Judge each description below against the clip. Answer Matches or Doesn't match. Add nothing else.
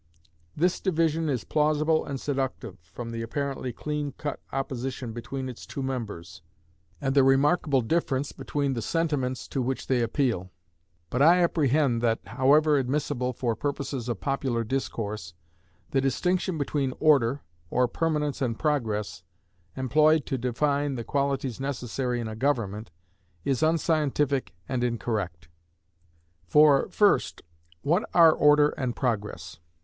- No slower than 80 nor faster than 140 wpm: Matches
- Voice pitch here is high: Doesn't match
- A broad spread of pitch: Doesn't match